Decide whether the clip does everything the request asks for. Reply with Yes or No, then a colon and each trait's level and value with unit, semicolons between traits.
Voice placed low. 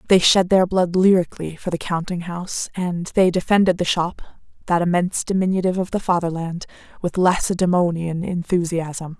No: medium, 175 Hz